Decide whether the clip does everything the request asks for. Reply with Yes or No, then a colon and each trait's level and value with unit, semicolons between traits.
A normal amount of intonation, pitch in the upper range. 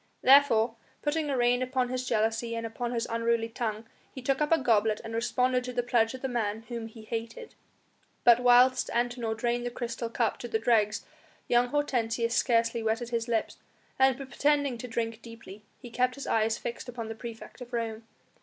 No: narrow, 1.8 semitones; high, 235 Hz